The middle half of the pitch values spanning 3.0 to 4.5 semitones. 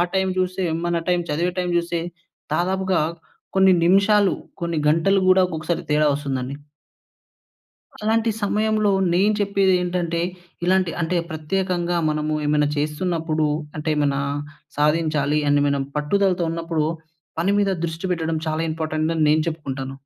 Yes: average, 3.5 semitones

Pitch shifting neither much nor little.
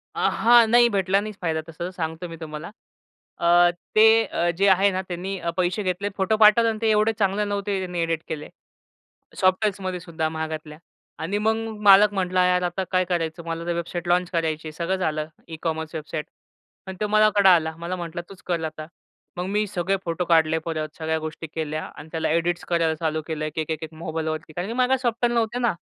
Yes: average, 3.7 semitones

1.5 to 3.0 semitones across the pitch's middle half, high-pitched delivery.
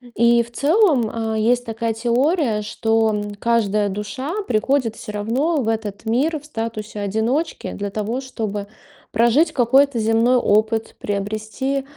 No: average, 3.4 semitones; high, 225 Hz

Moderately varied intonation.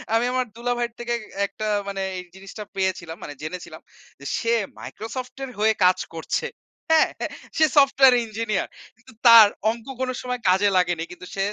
Yes: average, 4.5 semitones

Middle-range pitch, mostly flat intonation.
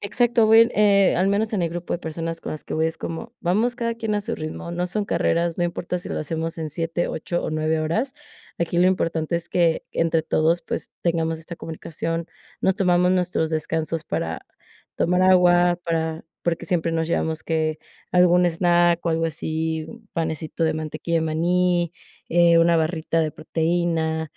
Yes: medium, 170 Hz; narrow, 1.9 semitones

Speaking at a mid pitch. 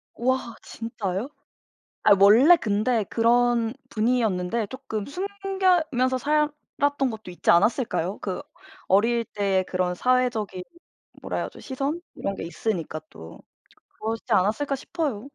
No: high, 230 Hz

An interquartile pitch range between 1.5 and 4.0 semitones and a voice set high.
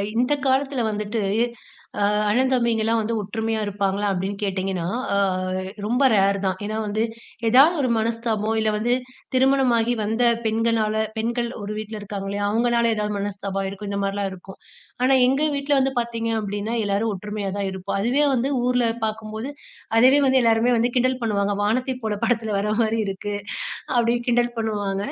Yes: average, 2.9 semitones; high, 220 Hz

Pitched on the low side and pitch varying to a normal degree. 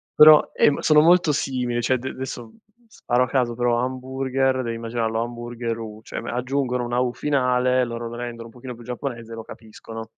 No: low, 120 Hz; narrow, 1.9 semitones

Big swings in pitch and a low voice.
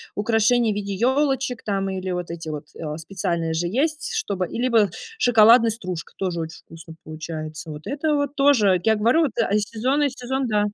No: wide, 6.6 semitones; high, 210 Hz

